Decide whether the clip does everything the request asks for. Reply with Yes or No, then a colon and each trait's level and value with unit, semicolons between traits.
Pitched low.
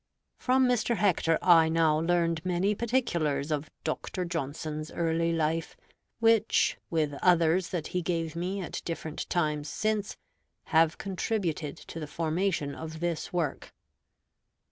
No: medium, 165 Hz